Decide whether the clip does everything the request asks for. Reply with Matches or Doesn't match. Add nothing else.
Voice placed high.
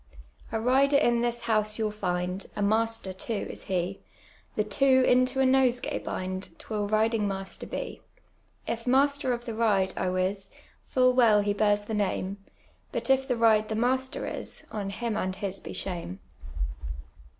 Matches